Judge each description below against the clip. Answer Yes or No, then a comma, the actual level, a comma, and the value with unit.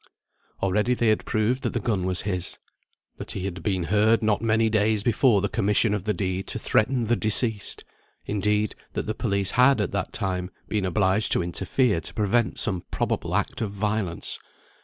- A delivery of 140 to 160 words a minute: No, average, 185 wpm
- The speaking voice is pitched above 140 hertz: No, low, 105 Hz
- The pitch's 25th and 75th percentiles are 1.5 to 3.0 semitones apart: Yes, narrow, 2.6 semitones